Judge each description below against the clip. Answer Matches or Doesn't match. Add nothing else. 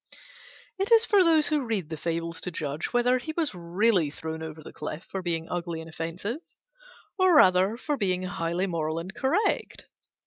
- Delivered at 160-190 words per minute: Matches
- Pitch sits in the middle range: Matches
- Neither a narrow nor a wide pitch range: Doesn't match